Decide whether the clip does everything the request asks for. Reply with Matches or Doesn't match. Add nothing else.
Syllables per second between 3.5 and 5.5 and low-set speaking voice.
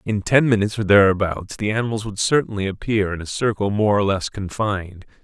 Doesn't match